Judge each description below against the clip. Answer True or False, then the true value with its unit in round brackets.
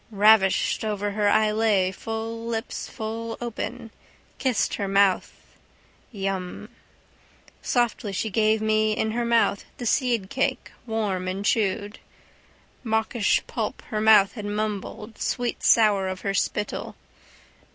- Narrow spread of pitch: True (2.1 semitones)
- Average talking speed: False (120 wpm)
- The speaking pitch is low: False (215 Hz)